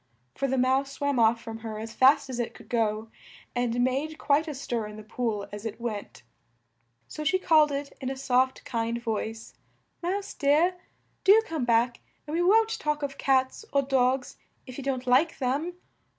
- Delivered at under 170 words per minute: No, average, 190 wpm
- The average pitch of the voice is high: Yes, very high, 260 Hz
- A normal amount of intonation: Yes, average, 3.9 semitones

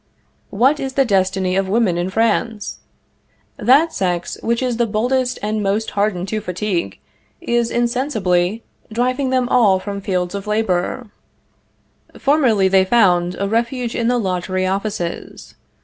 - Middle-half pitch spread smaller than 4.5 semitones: Yes, average, 4.1 semitones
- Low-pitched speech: No, high, 210 Hz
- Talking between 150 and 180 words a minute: No, average, 140 wpm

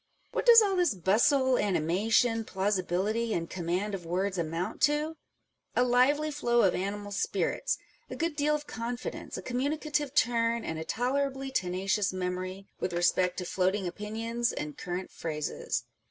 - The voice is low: No, high, 210 Hz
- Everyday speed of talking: Yes, average, 155 wpm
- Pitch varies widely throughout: Yes, wide, 6.1 semitones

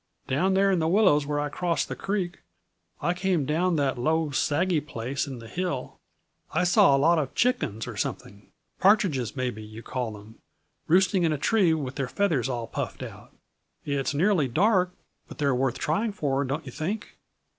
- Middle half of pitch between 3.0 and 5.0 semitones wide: No, wide, 5.6 semitones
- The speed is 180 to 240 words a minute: Yes, average, 185 wpm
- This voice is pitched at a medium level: Yes, medium, 150 Hz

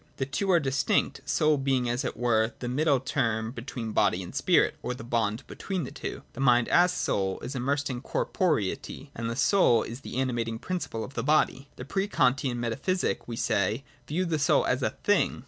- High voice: No, low, 130 Hz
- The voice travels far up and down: No, average, 3.8 semitones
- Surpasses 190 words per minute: Yes, average, 200 wpm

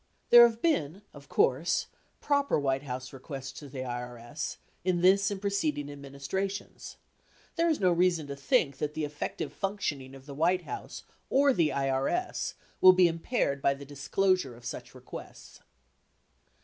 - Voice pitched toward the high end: No, medium, 150 Hz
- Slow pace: No, average, 155 wpm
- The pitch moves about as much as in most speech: No, wide, 5.8 semitones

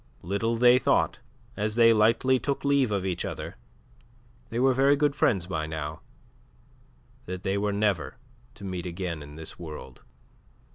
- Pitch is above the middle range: No, low, 100 Hz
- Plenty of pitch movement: Yes, wide, 5.7 semitones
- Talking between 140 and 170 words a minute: Yes, average, 155 wpm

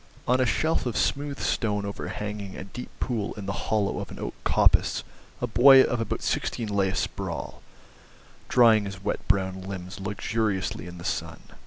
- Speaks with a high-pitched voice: No, low, 105 Hz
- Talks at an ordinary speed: Yes, average, 170 wpm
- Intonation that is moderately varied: Yes, average, 3.5 semitones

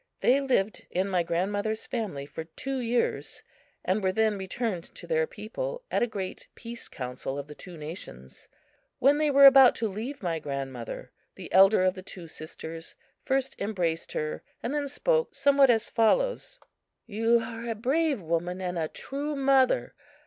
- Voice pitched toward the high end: Yes, high, 220 Hz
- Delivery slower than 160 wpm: No, average, 170 wpm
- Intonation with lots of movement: Yes, wide, 7.8 semitones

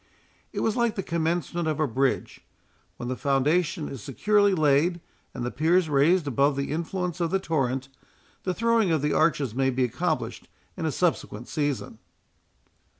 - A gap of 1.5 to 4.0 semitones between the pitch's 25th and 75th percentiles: No, average, 4.7 semitones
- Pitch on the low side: No, medium, 155 Hz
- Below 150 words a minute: No, average, 165 wpm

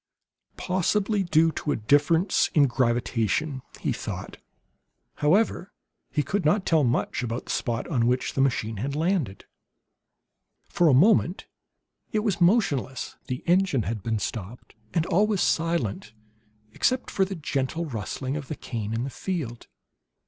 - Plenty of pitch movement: Yes, wide, 6.8 semitones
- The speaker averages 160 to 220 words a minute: No, average, 145 wpm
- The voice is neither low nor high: Yes, medium, 145 Hz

